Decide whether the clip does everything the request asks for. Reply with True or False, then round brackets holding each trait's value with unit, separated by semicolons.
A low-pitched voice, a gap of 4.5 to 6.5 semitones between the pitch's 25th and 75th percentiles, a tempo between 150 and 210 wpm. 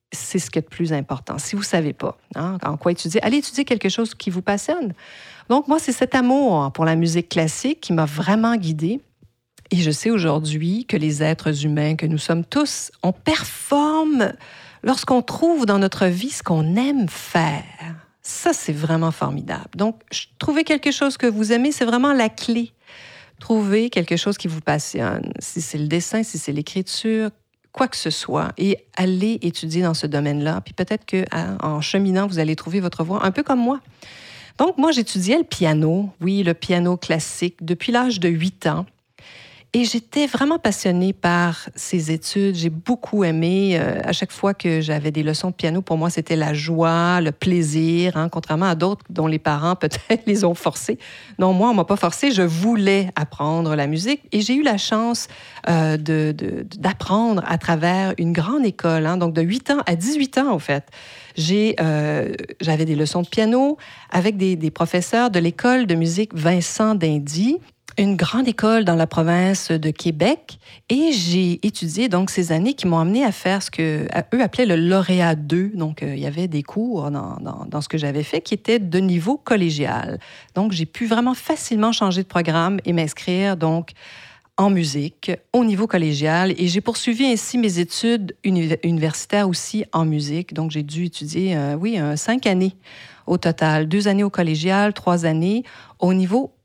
False (180 Hz; 5.2 semitones; 190 wpm)